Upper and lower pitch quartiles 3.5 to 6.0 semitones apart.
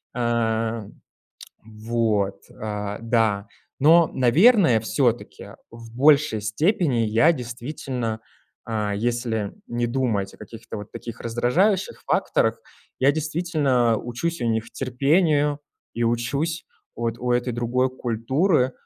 Yes: average, 4.0 semitones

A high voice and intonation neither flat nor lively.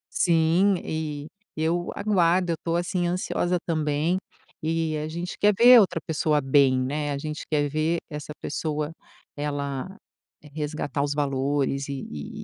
No: medium, 155 Hz; average, 3.0 semitones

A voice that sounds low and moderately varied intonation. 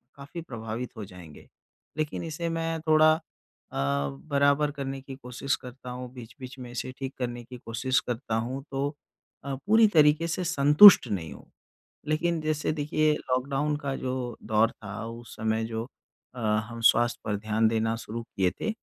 Yes: low, 125 Hz; average, 4.7 semitones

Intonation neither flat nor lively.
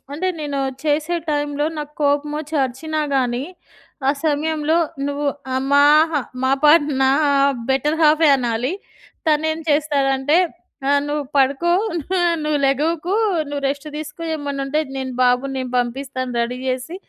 No: narrow, 2.3 semitones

